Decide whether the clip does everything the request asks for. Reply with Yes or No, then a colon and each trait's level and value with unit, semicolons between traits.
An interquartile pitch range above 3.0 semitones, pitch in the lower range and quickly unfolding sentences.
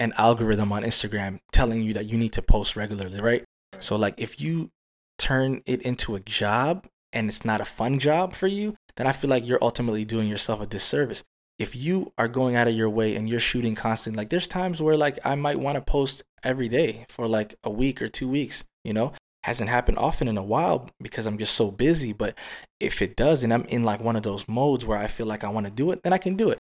Yes: average, 3.7 semitones; low, 115 Hz; fast, 250 wpm